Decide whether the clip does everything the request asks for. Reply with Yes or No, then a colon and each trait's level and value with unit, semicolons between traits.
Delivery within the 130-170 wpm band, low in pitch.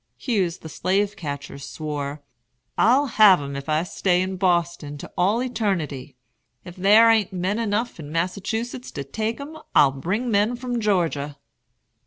No: average, 155 wpm; medium, 185 Hz